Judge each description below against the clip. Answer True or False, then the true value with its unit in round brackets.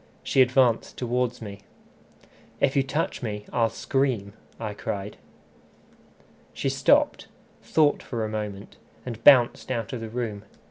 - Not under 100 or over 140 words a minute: True (135 wpm)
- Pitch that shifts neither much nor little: True (3.5 semitones)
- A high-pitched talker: False (115 Hz)